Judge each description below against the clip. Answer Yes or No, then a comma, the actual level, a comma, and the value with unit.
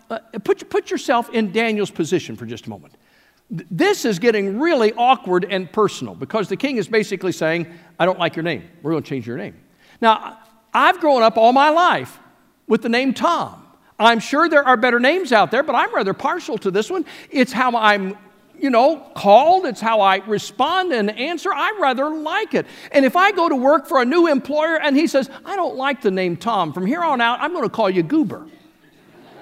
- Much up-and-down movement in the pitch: Yes, wide, 6.9 semitones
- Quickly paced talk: Yes, fast, 215 wpm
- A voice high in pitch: Yes, high, 235 Hz